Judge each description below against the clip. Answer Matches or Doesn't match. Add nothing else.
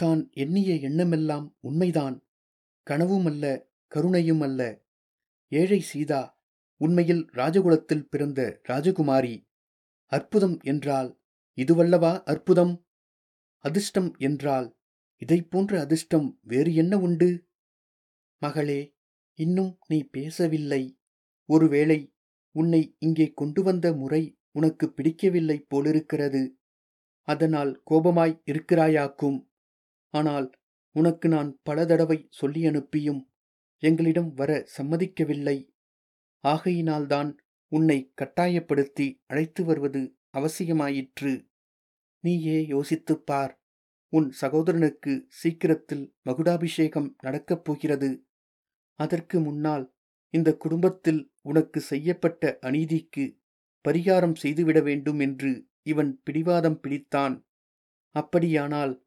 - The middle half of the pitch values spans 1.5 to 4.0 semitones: Matches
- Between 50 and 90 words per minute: Matches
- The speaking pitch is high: Doesn't match